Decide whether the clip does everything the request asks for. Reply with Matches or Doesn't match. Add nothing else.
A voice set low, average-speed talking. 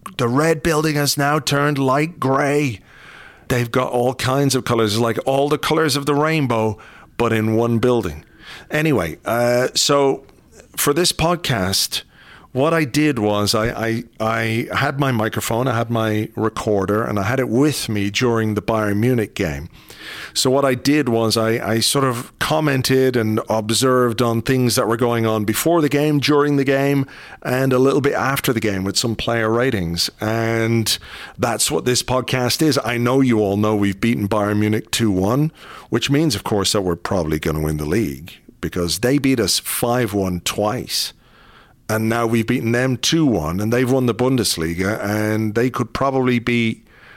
Matches